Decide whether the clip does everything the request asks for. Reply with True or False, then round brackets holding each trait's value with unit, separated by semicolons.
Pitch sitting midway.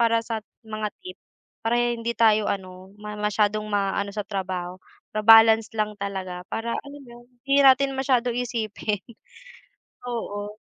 False (215 Hz)